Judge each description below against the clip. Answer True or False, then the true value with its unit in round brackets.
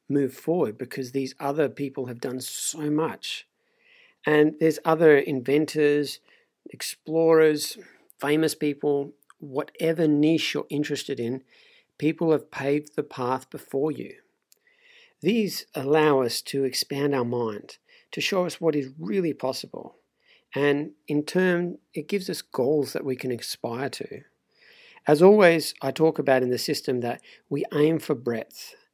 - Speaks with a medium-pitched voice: True (150 Hz)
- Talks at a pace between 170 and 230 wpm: False (140 wpm)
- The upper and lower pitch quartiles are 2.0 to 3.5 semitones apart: True (2.9 semitones)